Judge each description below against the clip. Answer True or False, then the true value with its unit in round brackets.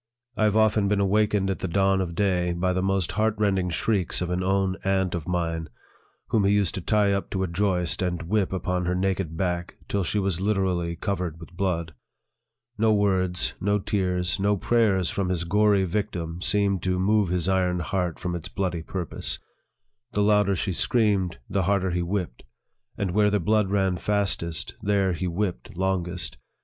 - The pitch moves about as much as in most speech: False (2.3 semitones)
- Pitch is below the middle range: True (95 Hz)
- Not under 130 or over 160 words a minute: False (185 wpm)